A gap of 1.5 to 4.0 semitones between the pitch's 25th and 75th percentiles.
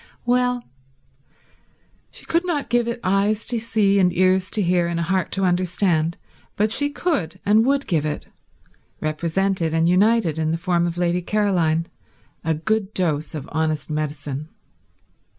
No: average, 4.9 semitones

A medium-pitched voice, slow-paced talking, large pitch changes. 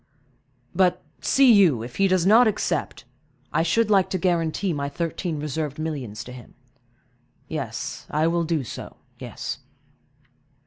Yes: medium, 160 Hz; slow, 130 wpm; wide, 6.0 semitones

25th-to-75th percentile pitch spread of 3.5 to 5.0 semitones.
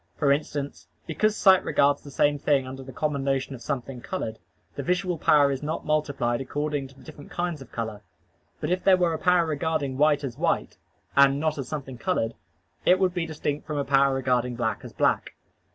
No: average, 2.9 semitones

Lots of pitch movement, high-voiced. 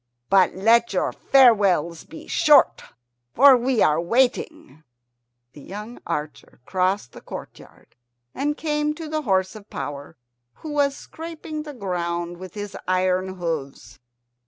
Yes: wide, 7.9 semitones; high, 200 Hz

